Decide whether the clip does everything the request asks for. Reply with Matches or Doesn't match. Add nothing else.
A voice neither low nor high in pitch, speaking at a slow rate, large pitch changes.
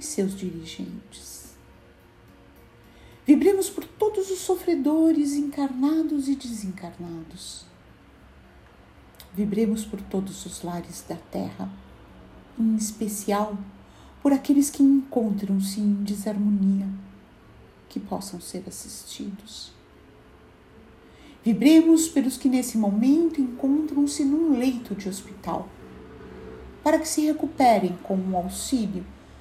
Doesn't match